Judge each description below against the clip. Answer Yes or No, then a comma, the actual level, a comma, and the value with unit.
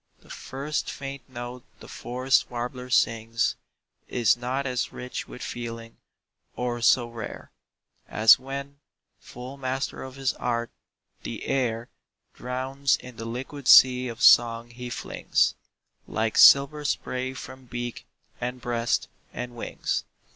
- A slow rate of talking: Yes, slow, 130 wpm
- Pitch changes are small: Yes, narrow, 1.8 semitones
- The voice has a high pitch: No, low, 125 Hz